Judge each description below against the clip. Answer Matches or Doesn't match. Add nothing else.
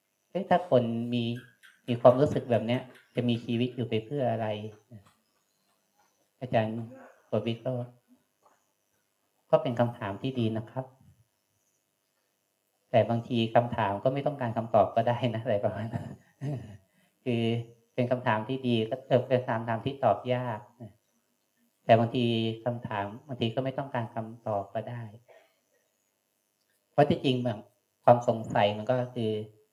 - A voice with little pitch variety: Matches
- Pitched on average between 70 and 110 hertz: Doesn't match